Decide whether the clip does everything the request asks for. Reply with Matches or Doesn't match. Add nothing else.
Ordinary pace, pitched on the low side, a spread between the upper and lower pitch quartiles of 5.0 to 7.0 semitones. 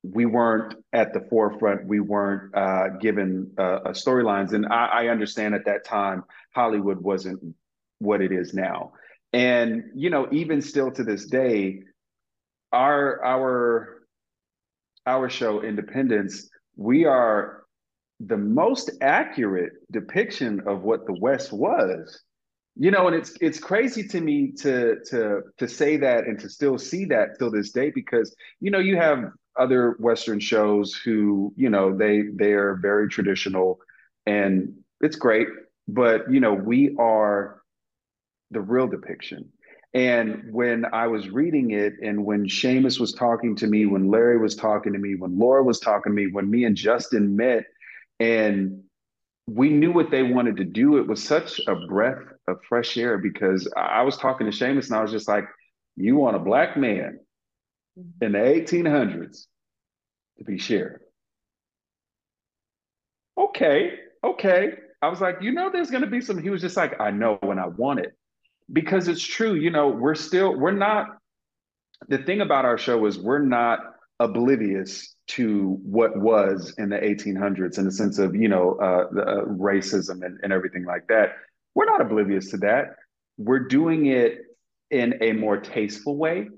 Matches